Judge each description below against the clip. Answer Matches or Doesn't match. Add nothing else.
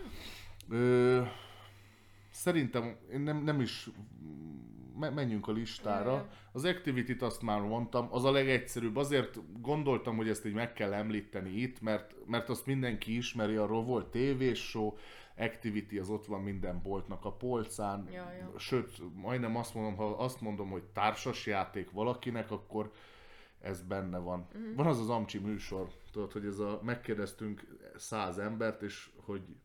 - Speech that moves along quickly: Doesn't match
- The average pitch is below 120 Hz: Matches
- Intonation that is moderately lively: Matches